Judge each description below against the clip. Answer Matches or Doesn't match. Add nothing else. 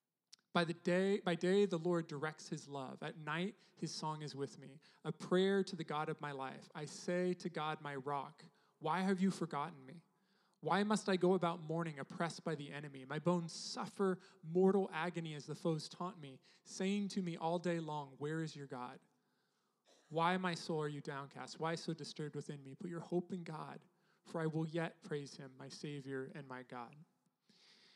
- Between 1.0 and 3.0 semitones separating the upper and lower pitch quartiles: Doesn't match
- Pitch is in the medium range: Matches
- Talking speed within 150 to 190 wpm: Doesn't match